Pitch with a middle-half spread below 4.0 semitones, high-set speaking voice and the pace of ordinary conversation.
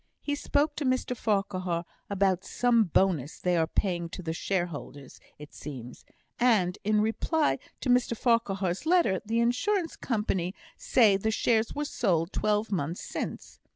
No: wide, 5.5 semitones; high, 205 Hz; average, 150 wpm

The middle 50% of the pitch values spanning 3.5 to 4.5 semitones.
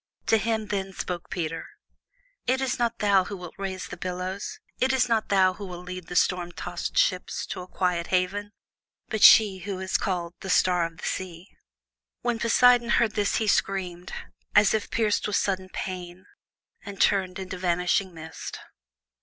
No: average, 2.7 semitones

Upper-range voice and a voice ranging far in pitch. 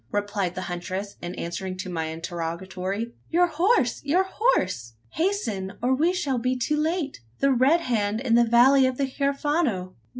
Yes: high, 235 Hz; wide, 7.7 semitones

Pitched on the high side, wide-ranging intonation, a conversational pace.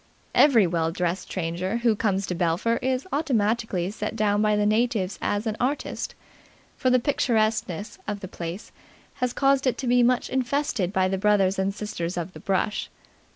No: high, 210 Hz; average, 4.5 semitones; average, 175 wpm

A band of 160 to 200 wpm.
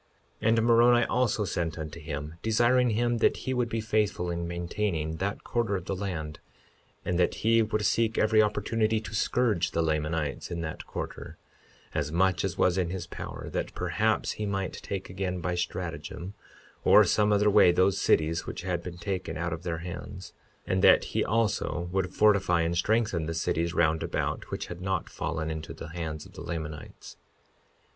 Yes: average, 185 wpm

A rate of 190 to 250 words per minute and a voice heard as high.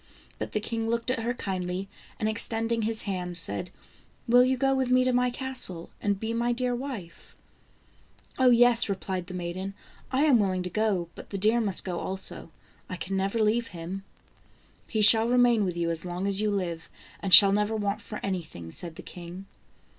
Yes: average, 200 wpm; high, 205 Hz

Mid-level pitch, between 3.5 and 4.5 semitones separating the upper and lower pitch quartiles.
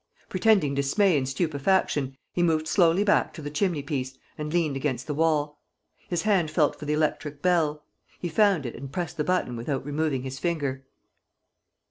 Yes: medium, 150 Hz; average, 3.9 semitones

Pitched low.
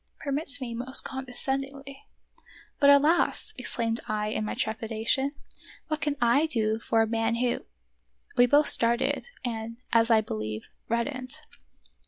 No: high, 235 Hz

